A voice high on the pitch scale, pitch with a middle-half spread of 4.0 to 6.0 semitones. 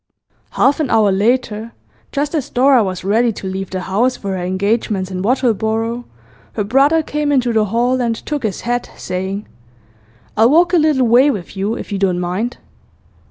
Yes: high, 225 Hz; average, 4.7 semitones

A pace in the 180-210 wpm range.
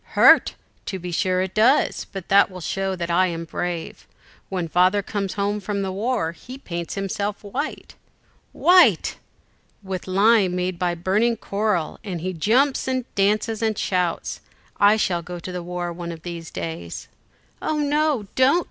No: average, 165 wpm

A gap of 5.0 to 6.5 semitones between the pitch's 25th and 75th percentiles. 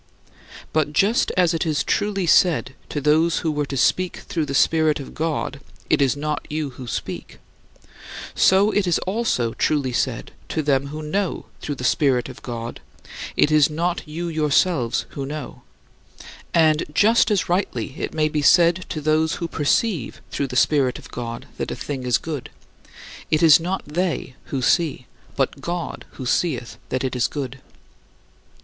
No: average, 3.8 semitones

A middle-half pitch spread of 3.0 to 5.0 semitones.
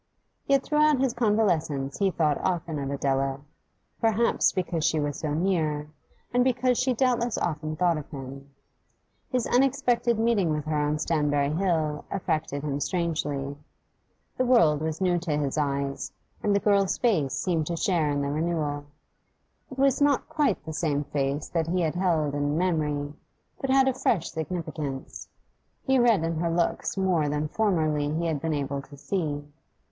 No: wide, 5.4 semitones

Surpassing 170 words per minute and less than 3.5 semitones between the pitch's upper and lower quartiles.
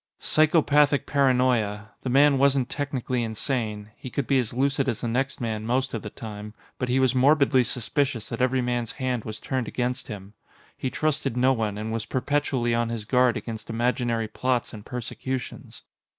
Yes: average, 180 wpm; average, 2.8 semitones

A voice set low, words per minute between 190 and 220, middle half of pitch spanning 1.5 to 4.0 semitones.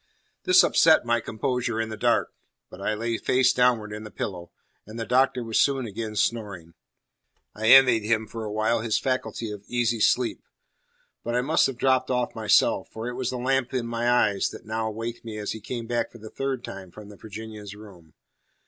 Yes: low, 115 Hz; fast, 205 wpm; narrow, 2.5 semitones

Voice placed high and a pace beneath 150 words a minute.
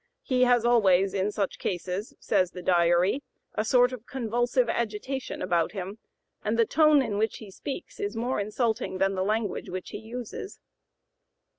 No: high, 215 Hz; average, 165 wpm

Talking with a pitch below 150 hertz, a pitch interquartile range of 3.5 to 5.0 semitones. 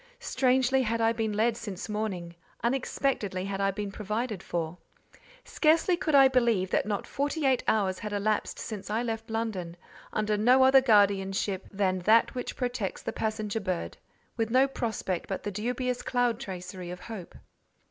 No: high, 215 Hz; average, 4.1 semitones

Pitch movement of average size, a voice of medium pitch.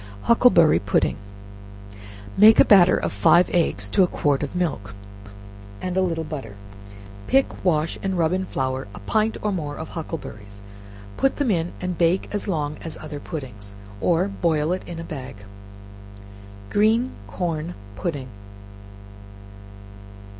Yes: average, 4.5 semitones; medium, 165 Hz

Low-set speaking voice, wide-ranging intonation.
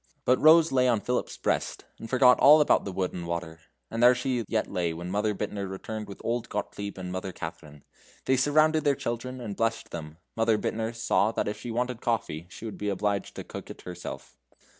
No: low, 110 Hz; average, 4.7 semitones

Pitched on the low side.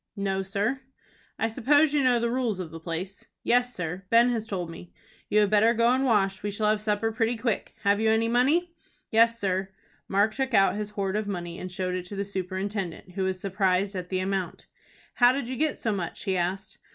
No: high, 205 Hz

